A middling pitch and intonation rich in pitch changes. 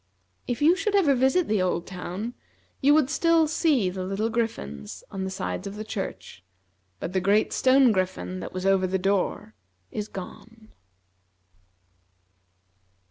No: high, 205 Hz; wide, 5.7 semitones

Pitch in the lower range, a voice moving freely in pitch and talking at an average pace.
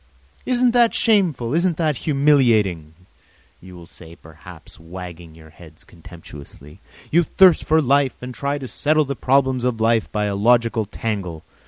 Yes: low, 115 Hz; wide, 8.8 semitones; average, 155 wpm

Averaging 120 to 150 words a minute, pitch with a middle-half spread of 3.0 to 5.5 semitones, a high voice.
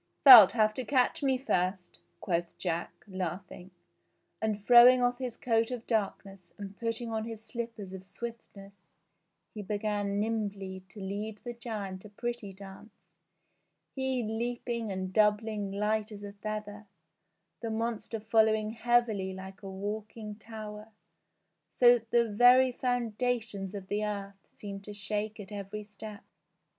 No: average, 140 wpm; narrow, 2.5 semitones; high, 215 Hz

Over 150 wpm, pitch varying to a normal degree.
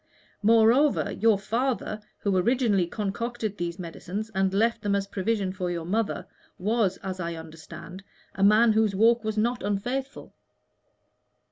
No: average, 145 wpm; average, 3.4 semitones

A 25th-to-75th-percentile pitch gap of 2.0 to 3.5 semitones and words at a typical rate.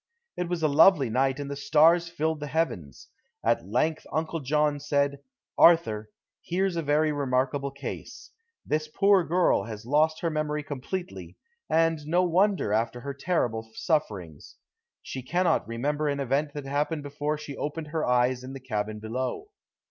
No: average, 3.9 semitones; average, 160 wpm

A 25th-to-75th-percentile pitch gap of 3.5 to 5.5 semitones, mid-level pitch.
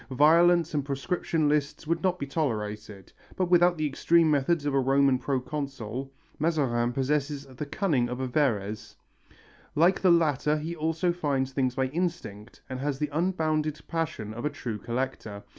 Yes: average, 3.9 semitones; medium, 145 Hz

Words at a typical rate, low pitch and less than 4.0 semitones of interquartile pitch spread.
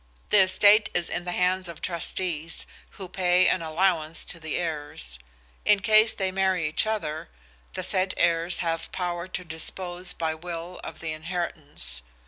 No: average, 160 wpm; medium, 175 Hz; narrow, 2.5 semitones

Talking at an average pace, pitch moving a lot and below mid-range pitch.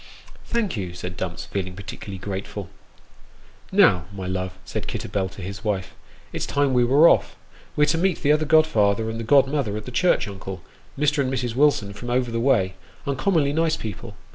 Yes: average, 195 wpm; wide, 6.8 semitones; low, 115 Hz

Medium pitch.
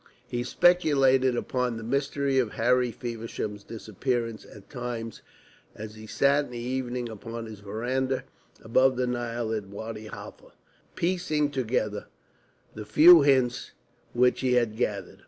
No: low, 120 Hz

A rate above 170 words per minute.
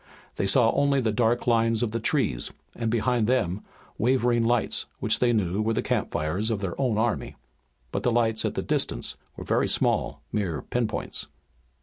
Yes: average, 185 wpm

